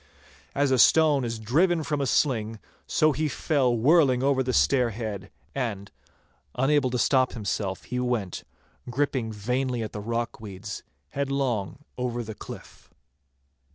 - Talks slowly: No, average, 145 wpm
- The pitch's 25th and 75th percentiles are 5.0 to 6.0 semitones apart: No, average, 3.8 semitones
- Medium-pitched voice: No, low, 125 Hz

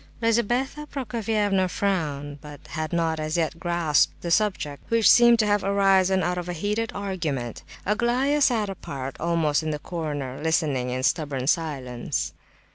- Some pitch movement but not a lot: No, wide, 5.9 semitones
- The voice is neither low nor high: Yes, medium, 175 Hz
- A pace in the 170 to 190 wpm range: No, average, 150 wpm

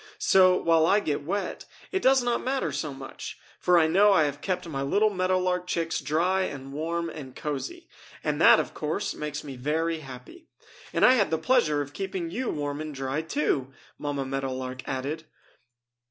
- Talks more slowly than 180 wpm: No, average, 190 wpm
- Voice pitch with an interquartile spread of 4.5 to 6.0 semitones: Yes, average, 4.8 semitones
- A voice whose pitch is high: No, medium, 160 Hz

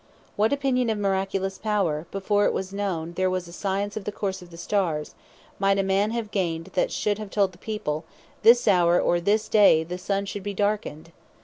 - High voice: Yes, high, 195 Hz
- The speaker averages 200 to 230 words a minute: Yes, fast, 205 wpm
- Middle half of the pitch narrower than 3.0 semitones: Yes, narrow, 2.6 semitones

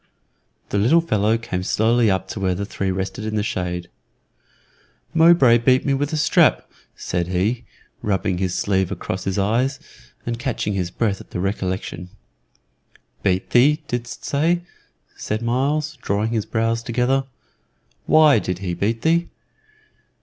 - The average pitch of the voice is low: Yes, low, 110 Hz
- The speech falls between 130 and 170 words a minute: Yes, average, 150 wpm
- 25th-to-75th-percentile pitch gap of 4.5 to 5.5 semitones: Yes, average, 5.2 semitones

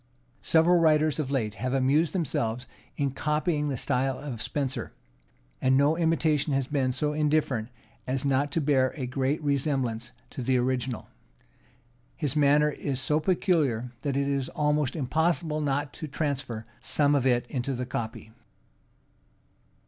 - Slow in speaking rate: No, average, 150 wpm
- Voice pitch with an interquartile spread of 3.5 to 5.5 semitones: No, average, 2.7 semitones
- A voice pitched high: No, medium, 140 Hz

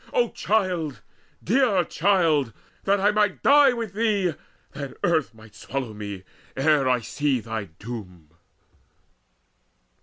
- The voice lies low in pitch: No, medium, 150 Hz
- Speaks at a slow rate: Yes, slow, 120 wpm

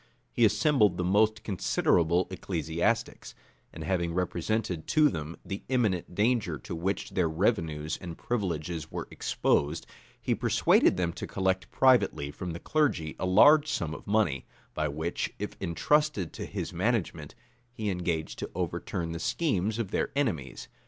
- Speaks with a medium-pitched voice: No, very low, 90 Hz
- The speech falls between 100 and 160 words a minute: Yes, average, 150 wpm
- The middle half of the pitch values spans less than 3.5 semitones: No, average, 4.9 semitones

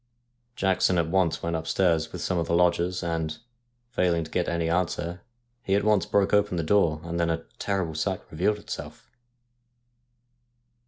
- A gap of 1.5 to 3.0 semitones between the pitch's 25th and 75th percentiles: Yes, narrow, 2.4 semitones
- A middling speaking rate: Yes, average, 165 wpm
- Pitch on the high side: No, very low, 85 Hz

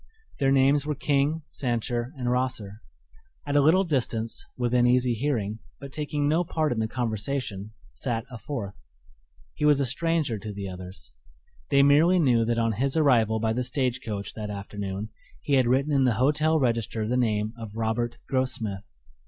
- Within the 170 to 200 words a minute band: Yes, average, 175 wpm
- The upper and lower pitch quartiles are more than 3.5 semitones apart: Yes, average, 4.1 semitones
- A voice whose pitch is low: Yes, low, 125 Hz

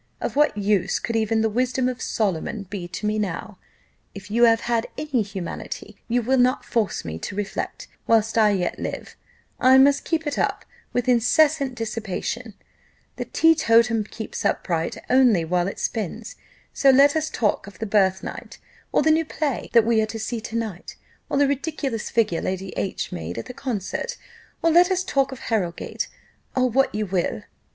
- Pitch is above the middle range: Yes, high, 225 Hz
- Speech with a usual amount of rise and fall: Yes, average, 4.5 semitones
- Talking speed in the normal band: Yes, average, 180 wpm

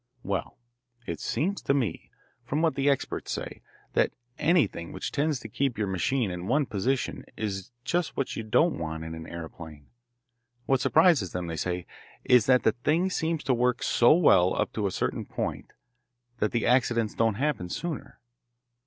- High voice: No, low, 120 Hz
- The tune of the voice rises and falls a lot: Yes, wide, 7.3 semitones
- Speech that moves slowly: No, average, 175 wpm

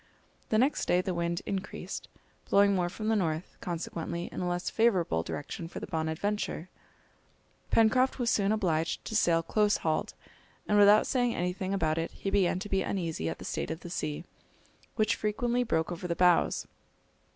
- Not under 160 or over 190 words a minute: Yes, average, 175 wpm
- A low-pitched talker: No, medium, 185 Hz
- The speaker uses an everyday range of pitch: Yes, average, 4.0 semitones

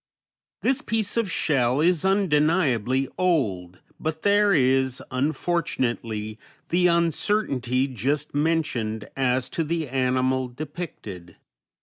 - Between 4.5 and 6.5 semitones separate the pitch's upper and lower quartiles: Yes, average, 5.2 semitones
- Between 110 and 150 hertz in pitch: Yes, medium, 140 Hz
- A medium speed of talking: No, slow, 100 wpm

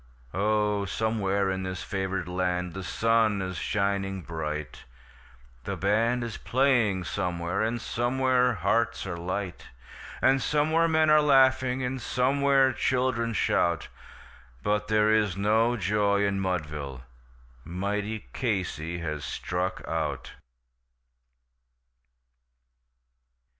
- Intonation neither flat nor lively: Yes, average, 4.7 semitones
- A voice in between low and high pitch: No, low, 105 Hz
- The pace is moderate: No, slow, 105 wpm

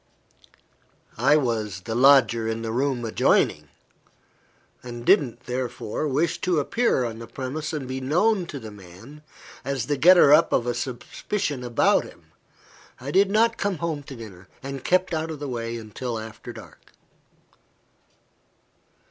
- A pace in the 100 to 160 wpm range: Yes, average, 150 wpm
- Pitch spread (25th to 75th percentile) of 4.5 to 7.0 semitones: Yes, average, 4.9 semitones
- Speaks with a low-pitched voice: Yes, low, 130 Hz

